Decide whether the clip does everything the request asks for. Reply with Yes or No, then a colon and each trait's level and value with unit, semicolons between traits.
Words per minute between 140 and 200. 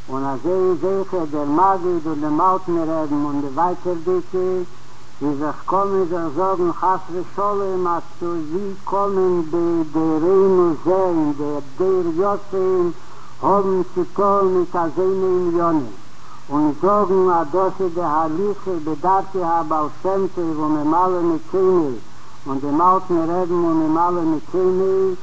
Yes: average, 145 wpm